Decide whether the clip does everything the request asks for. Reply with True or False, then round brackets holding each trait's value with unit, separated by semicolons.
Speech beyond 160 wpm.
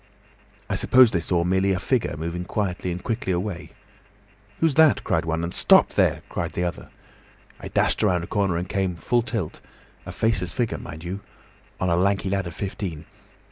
True (180 wpm)